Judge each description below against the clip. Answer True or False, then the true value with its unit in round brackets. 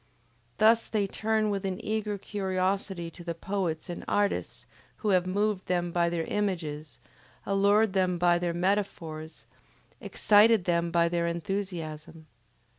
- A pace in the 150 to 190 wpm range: False (135 wpm)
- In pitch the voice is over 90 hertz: True (185 Hz)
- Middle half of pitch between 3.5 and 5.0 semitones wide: False (3.1 semitones)